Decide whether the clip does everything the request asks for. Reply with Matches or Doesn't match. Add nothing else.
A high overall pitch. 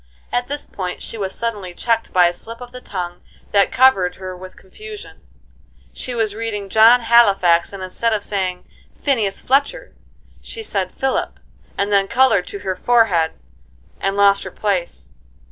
Matches